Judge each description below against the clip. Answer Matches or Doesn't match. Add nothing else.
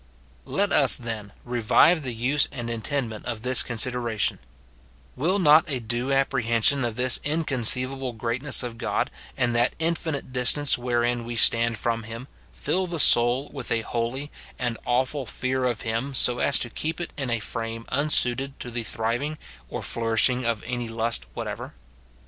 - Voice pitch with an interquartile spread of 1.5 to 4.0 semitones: Matches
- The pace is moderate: Matches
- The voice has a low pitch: Matches